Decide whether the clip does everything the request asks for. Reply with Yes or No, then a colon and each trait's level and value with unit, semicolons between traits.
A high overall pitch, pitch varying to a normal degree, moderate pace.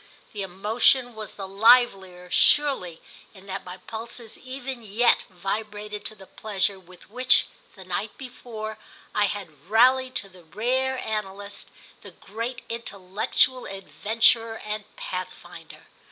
No: high, 215 Hz; average, 3.8 semitones; slow, 125 wpm